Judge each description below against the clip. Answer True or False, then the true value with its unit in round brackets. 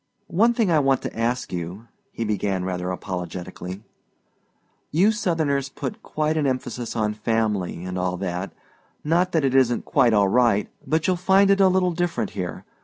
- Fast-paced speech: False (175 wpm)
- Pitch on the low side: True (125 Hz)